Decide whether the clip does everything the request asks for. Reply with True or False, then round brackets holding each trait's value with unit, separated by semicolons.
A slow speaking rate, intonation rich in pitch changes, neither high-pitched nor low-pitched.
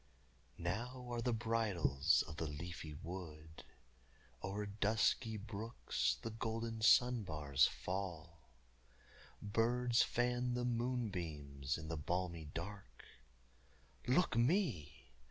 False (100 wpm; 6.7 semitones; 100 Hz)